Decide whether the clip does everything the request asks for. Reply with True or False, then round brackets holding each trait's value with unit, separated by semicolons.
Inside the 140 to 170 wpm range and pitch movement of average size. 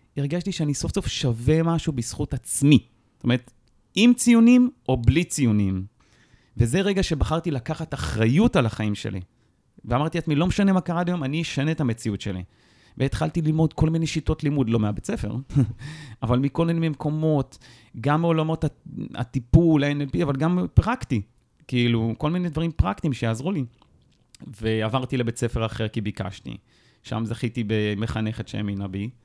False (150 wpm; 5.7 semitones)